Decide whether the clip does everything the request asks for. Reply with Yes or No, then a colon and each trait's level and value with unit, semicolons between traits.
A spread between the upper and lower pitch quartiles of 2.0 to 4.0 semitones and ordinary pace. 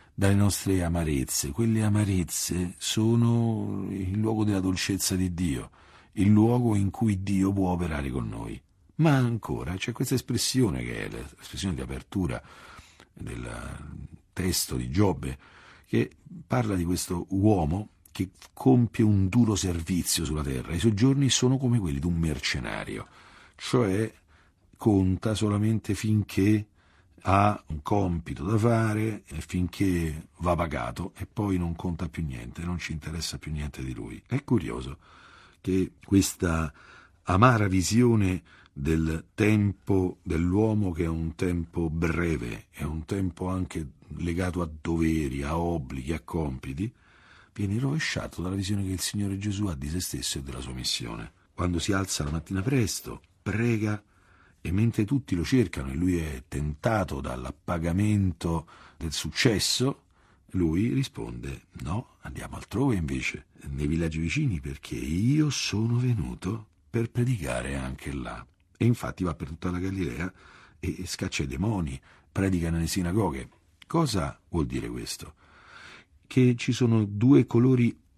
No: average, 4.9 semitones; average, 140 wpm